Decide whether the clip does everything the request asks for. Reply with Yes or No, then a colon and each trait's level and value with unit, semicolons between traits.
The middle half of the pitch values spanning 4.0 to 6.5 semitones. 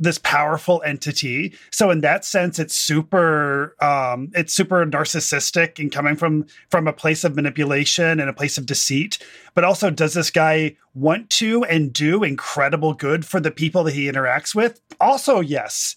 No: average, 3.3 semitones